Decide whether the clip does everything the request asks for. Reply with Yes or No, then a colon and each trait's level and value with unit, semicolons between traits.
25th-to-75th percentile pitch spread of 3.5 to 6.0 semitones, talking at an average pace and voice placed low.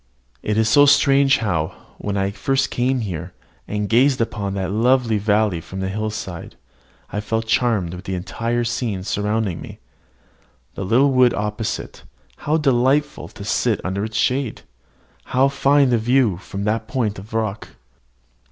Yes: average, 4.1 semitones; average, 155 wpm; low, 110 Hz